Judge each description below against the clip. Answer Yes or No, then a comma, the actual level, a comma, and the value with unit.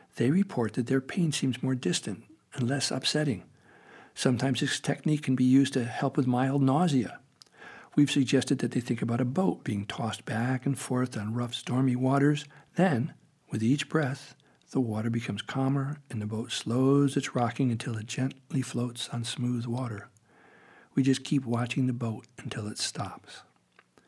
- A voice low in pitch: Yes, low, 130 Hz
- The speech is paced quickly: No, average, 170 wpm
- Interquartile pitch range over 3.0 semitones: No, narrow, 2.6 semitones